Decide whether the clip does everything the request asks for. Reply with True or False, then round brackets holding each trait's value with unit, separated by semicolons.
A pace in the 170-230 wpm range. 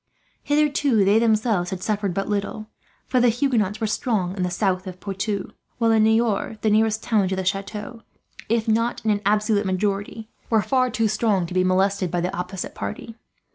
True (200 wpm)